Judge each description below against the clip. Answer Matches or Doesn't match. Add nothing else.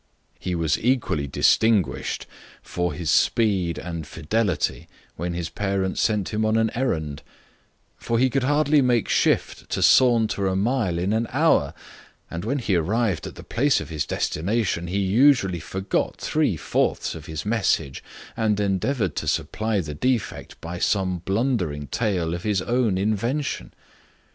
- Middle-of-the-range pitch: Doesn't match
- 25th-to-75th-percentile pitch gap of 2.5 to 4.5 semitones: Doesn't match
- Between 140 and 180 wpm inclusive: Matches